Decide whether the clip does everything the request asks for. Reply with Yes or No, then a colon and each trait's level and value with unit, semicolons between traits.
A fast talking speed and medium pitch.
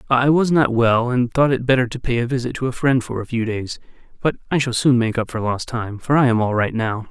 No: fast, 285 wpm; low, 120 Hz